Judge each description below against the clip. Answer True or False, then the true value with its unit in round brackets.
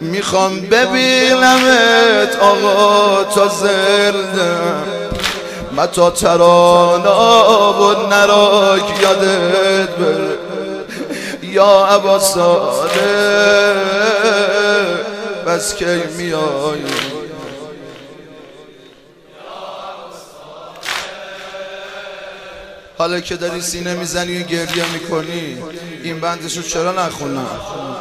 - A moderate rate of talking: False (60 wpm)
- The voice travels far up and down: False (2.8 semitones)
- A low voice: False (195 Hz)